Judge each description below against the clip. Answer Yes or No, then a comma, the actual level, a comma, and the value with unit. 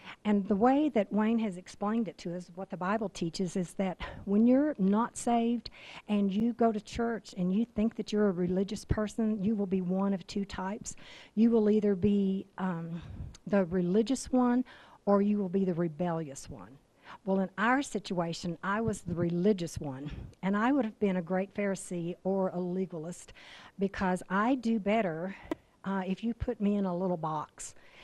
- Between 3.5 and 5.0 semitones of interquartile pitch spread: No, average, 2.9 semitones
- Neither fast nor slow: Yes, average, 190 wpm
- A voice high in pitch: Yes, high, 200 Hz